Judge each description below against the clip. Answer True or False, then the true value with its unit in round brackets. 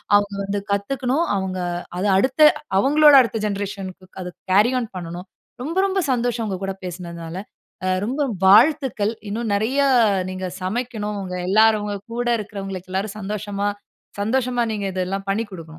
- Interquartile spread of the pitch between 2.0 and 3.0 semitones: False (4.0 semitones)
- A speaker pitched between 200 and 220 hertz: True (205 Hz)